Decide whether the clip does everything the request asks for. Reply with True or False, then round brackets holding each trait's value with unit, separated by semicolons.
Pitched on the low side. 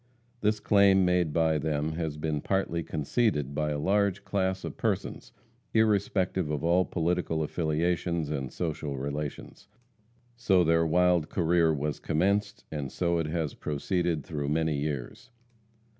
True (80 Hz)